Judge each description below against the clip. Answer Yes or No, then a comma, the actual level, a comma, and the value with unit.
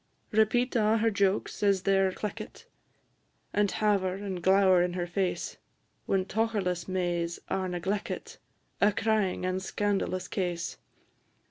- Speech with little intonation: Yes, narrow, 2.2 semitones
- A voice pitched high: Yes, high, 195 Hz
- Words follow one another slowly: Yes, slow, 130 wpm